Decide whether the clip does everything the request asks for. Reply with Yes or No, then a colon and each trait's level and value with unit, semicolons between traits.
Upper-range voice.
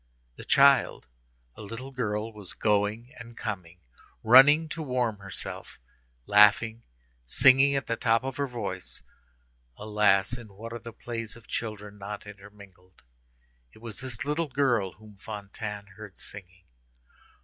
No: low, 110 Hz